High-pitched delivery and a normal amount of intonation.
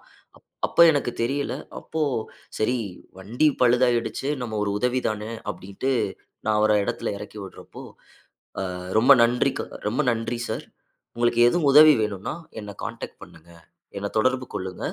No: low, 115 Hz; average, 3.4 semitones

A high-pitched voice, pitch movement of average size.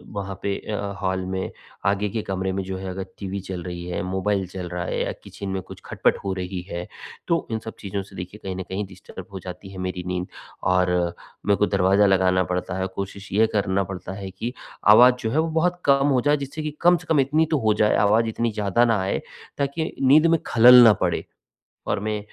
No: low, 100 Hz; average, 3.3 semitones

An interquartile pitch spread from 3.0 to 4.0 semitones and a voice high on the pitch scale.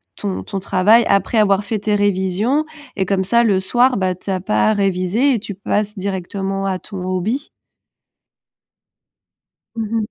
No: narrow, 2.6 semitones; high, 195 Hz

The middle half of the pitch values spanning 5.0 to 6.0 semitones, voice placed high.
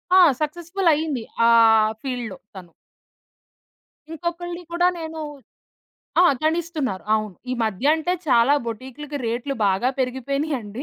Yes: wide, 5.5 semitones; very high, 280 Hz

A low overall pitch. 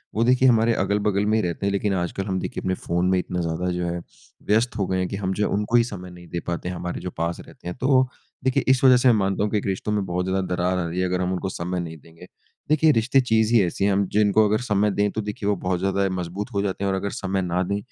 Yes: very low, 95 Hz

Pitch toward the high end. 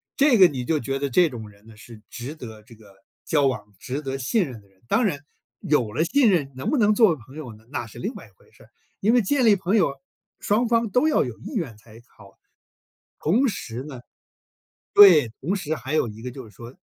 No: medium, 140 Hz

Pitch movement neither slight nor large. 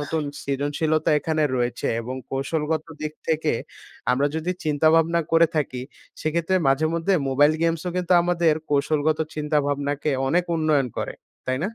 No: narrow, 2.3 semitones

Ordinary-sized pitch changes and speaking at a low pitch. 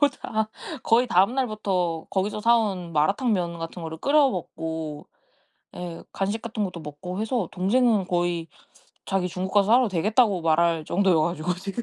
No: average, 4.3 semitones; high, 190 Hz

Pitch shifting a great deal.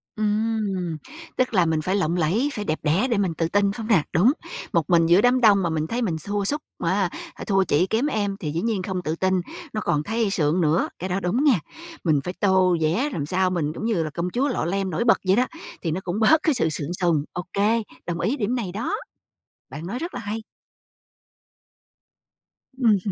No: average, 4.7 semitones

